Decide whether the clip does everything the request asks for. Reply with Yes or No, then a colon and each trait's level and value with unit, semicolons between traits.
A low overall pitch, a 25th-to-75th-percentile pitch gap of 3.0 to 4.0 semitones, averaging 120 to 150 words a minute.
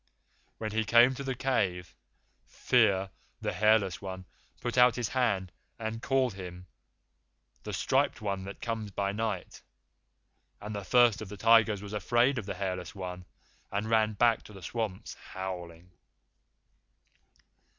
Yes: low, 105 Hz; average, 3.4 semitones; average, 145 wpm